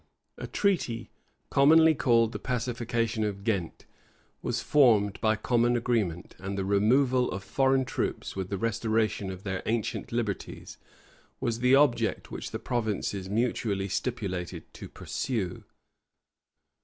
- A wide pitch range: No, average, 3.8 semitones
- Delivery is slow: Yes, slow, 130 wpm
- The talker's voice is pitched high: No, low, 115 Hz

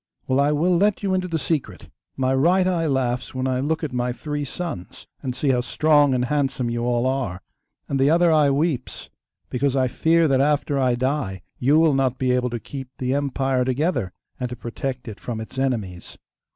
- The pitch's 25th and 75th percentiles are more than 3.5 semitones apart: No, average, 3.2 semitones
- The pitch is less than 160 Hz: Yes, low, 135 Hz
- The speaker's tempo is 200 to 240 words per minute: Yes, fast, 205 wpm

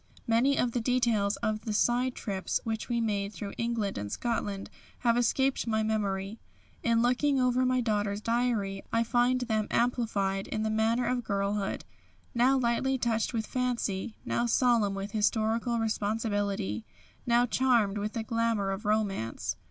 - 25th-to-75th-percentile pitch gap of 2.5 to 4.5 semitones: Yes, average, 2.8 semitones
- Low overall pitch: No, high, 225 Hz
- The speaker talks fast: No, average, 155 wpm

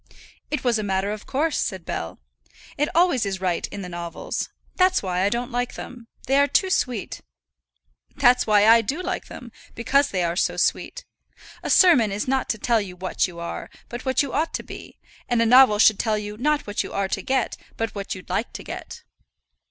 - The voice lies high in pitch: Yes, high, 230 Hz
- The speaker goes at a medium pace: No, fast, 215 wpm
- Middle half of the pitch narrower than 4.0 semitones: No, average, 5.1 semitones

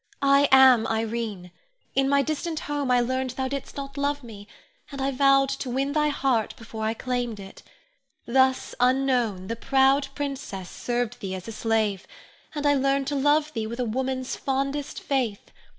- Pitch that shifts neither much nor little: Yes, average, 3.4 semitones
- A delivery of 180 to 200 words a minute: No, average, 170 wpm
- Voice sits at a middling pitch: No, very high, 260 Hz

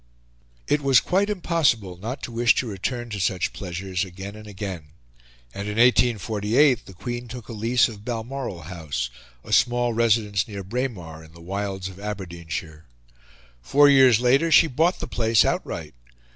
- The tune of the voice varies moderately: Yes, average, 4.7 semitones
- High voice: No, low, 110 Hz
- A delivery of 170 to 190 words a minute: No, average, 160 wpm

